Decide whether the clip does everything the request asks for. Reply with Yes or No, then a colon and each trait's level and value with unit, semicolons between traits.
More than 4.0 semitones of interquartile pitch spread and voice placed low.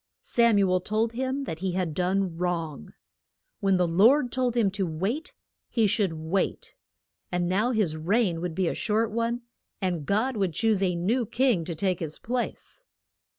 No: average, 4.7 semitones; high, 195 Hz